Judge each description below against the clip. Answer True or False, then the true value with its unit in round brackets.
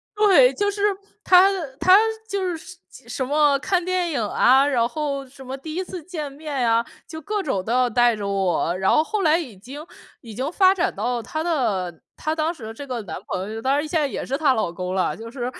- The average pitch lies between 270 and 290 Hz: True (275 Hz)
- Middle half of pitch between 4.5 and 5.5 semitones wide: False (6.3 semitones)